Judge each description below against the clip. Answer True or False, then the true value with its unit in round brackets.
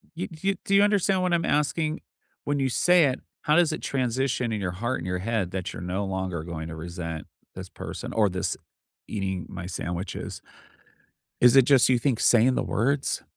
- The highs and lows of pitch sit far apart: True (8.2 semitones)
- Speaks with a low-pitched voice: True (120 Hz)